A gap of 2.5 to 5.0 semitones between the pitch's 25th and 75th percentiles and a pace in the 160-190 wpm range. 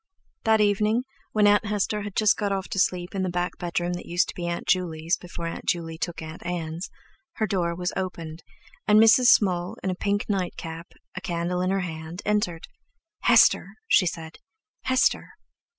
Yes: average, 3.1 semitones; average, 185 wpm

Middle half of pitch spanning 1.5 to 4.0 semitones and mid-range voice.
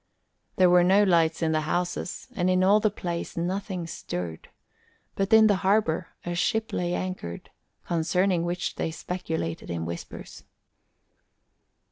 Yes: narrow, 2.6 semitones; medium, 180 Hz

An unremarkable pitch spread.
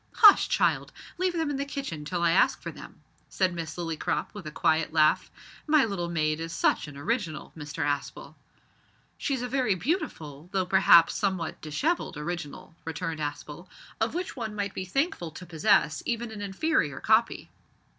No: wide, 6.9 semitones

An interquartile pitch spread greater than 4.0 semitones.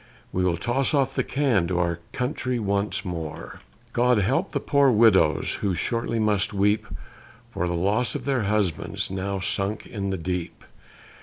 Yes: average, 4.6 semitones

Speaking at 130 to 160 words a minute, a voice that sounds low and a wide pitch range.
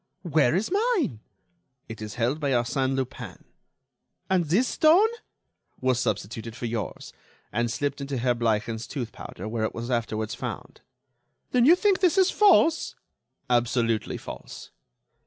Yes: average, 140 wpm; low, 130 Hz; wide, 9.0 semitones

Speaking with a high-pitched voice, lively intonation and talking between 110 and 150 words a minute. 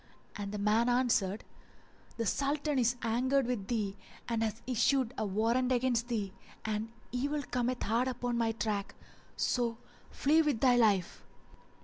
No: high, 235 Hz; average, 2.7 semitones; average, 145 wpm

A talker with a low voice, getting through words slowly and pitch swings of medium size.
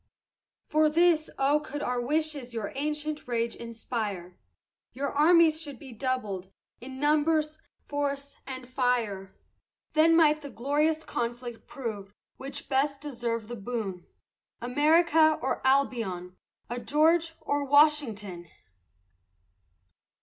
No: very high, 275 Hz; slow, 115 wpm; average, 4.4 semitones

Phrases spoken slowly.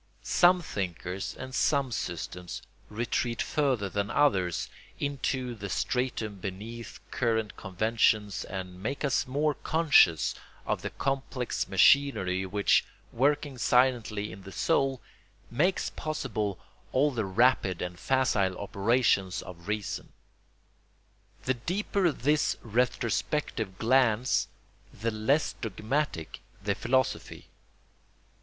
Yes: slow, 105 wpm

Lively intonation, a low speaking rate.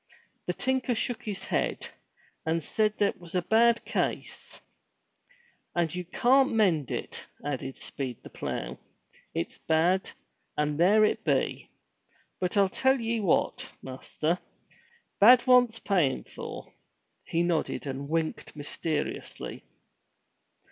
Yes: wide, 6.5 semitones; slow, 120 wpm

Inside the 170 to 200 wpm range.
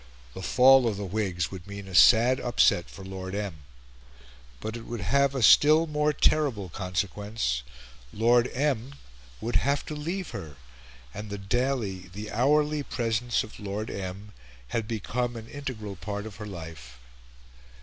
No: average, 155 wpm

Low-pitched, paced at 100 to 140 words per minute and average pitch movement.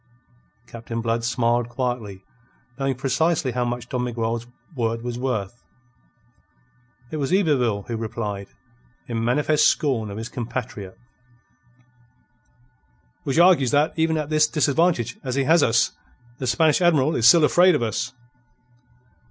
Yes: low, 125 Hz; slow, 135 wpm; average, 4.4 semitones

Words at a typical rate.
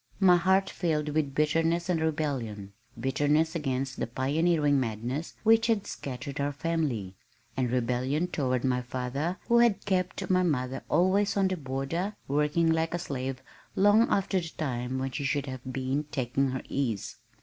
Yes: average, 160 wpm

